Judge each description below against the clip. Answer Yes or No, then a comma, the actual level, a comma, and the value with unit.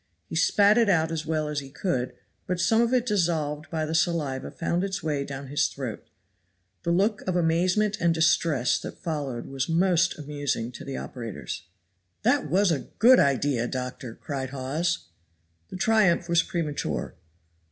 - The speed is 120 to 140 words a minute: No, average, 165 wpm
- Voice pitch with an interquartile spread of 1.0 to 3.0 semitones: No, average, 4.4 semitones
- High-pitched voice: No, medium, 160 Hz